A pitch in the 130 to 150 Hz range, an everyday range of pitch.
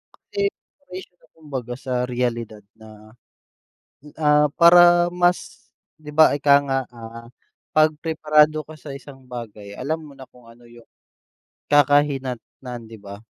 Yes: medium, 140 Hz; average, 4.7 semitones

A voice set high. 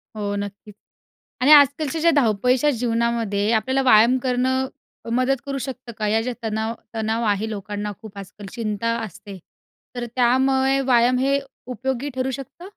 Yes: high, 235 Hz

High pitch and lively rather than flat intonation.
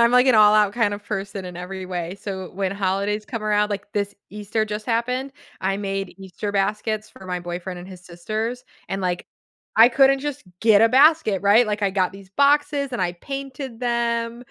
No: high, 210 Hz; average, 3.5 semitones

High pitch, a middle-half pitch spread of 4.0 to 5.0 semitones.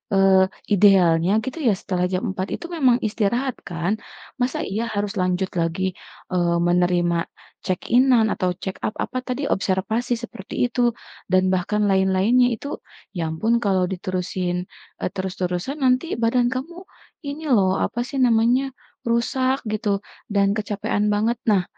Yes: high, 205 Hz; average, 4.5 semitones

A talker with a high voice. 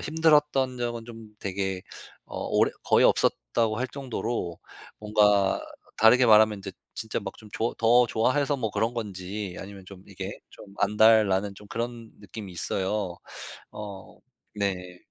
No: low, 105 Hz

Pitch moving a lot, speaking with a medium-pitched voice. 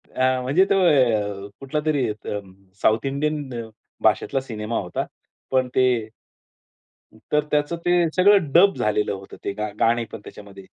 No: wide, 6.0 semitones; low, 130 Hz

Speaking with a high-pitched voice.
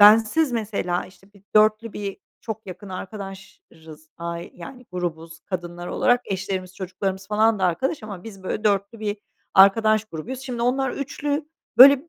Yes: high, 200 Hz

